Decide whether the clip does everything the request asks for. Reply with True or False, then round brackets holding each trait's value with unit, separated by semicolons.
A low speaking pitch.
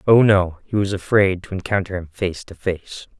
True (95 Hz)